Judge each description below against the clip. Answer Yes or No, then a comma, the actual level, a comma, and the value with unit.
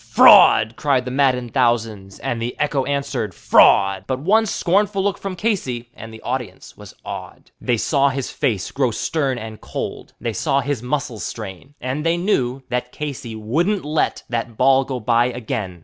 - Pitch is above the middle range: No, low, 125 Hz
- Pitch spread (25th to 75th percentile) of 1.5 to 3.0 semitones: No, average, 3.9 semitones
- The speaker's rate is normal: Yes, average, 175 wpm